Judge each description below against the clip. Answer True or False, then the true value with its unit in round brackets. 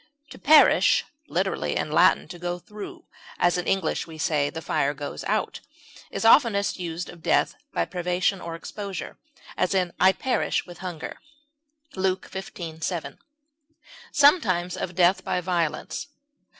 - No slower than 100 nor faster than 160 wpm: True (140 wpm)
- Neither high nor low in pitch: True (180 Hz)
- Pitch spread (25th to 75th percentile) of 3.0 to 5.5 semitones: False (2.5 semitones)